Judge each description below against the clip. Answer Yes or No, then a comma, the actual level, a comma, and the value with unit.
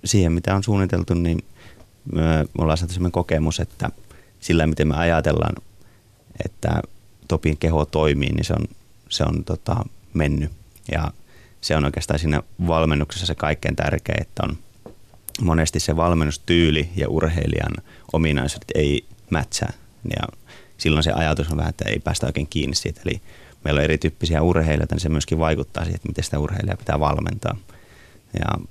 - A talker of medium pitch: No, very low, 80 Hz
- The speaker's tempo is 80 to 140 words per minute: No, fast, 155 wpm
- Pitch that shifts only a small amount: No, average, 3.9 semitones